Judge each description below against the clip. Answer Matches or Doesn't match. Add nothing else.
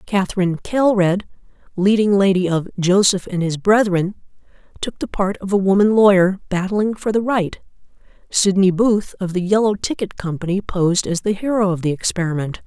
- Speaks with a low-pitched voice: Doesn't match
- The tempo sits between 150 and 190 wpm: Matches